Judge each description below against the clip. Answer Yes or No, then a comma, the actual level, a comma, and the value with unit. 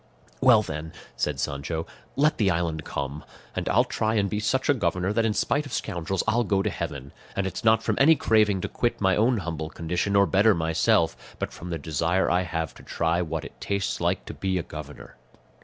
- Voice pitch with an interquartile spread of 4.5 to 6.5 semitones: Yes, average, 4.9 semitones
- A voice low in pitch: Yes, very low, 90 Hz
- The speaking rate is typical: No, fast, 215 wpm